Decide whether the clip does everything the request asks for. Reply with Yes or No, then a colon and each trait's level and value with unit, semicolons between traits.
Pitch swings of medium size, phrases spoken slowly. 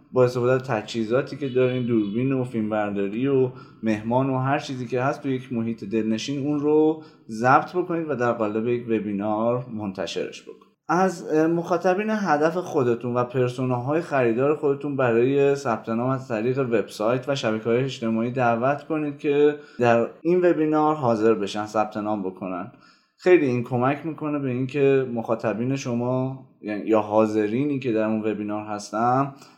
No: average, 4.1 semitones; fast, 155 wpm